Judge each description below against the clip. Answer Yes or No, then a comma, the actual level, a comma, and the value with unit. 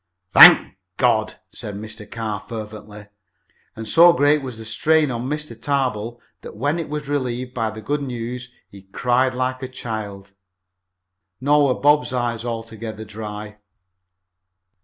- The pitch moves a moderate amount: Yes, average, 3.8 semitones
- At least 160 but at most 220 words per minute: No, average, 140 wpm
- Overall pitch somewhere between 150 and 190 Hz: No, low, 120 Hz